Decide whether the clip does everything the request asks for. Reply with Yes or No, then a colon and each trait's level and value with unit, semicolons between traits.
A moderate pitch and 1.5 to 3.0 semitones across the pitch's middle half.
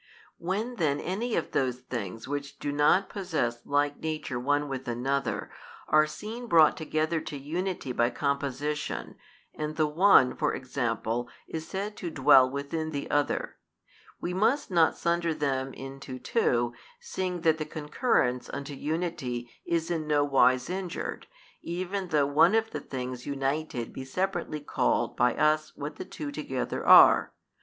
No: medium, 150 Hz; average, 4.2 semitones